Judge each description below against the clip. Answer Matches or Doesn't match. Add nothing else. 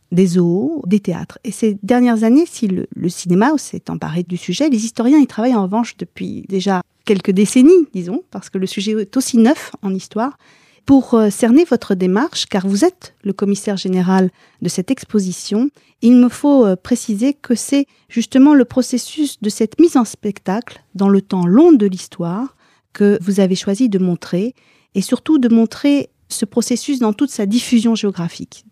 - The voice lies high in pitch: Matches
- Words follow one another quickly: Doesn't match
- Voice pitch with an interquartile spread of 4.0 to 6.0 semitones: Matches